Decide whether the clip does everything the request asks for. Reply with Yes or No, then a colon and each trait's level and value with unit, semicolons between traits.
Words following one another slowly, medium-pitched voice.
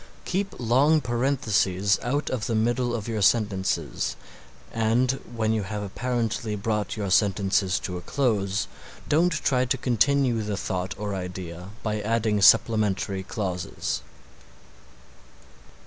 No: slow, 125 wpm; low, 110 Hz